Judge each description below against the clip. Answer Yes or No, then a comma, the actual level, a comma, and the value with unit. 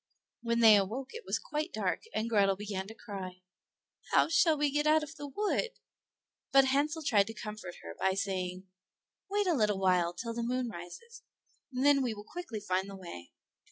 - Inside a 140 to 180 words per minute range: No, average, 195 wpm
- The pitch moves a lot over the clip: Yes, wide, 7.0 semitones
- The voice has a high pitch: Yes, high, 225 Hz